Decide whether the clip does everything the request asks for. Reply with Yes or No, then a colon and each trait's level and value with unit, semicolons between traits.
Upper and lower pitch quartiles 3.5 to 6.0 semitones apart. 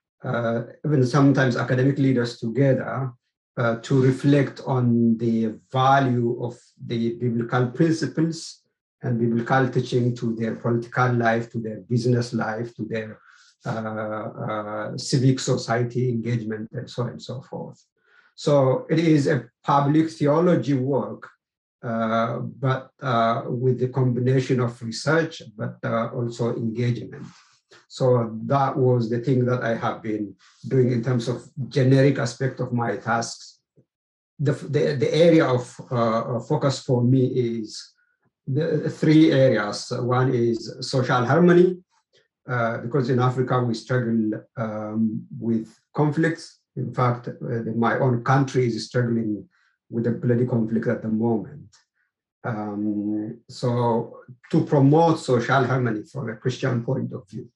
No: average, 2.8 semitones